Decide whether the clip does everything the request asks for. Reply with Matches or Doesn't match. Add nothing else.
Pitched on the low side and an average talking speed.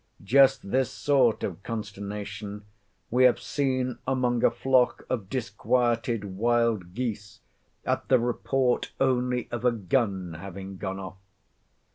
Doesn't match